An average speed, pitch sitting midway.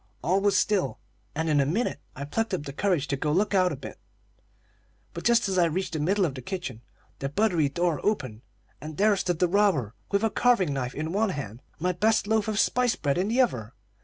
No: fast, 230 wpm; medium, 180 Hz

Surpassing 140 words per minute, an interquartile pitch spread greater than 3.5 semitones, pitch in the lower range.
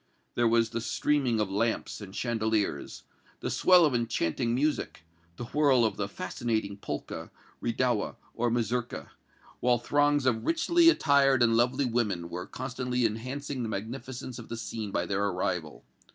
No: average, 150 wpm; average, 3.2 semitones; low, 120 Hz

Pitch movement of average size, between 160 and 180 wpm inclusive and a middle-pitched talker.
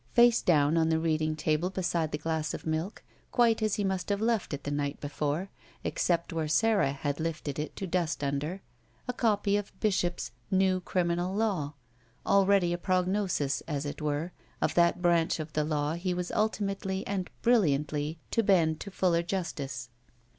Yes: average, 4.2 semitones; average, 175 wpm; medium, 170 Hz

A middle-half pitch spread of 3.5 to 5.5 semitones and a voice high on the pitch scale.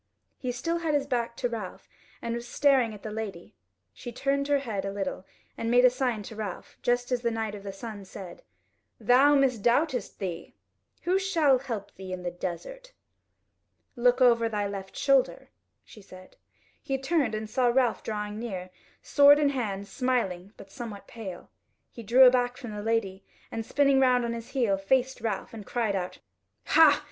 Yes: average, 4.5 semitones; high, 235 Hz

